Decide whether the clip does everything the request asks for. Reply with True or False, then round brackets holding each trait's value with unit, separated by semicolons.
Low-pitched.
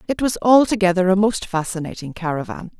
False (190 Hz)